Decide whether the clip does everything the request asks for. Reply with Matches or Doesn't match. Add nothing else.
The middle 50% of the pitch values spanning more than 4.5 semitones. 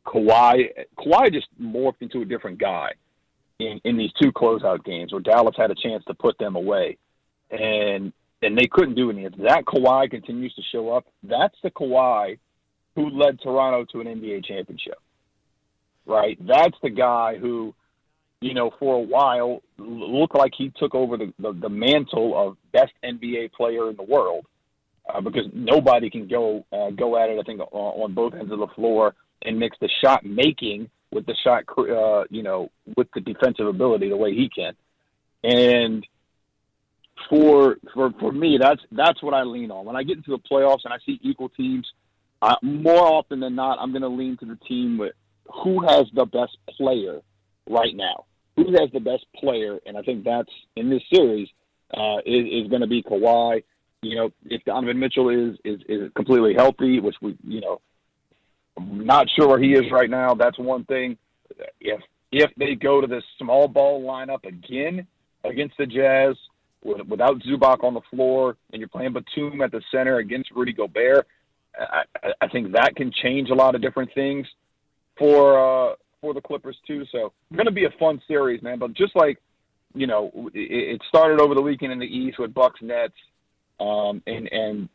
Doesn't match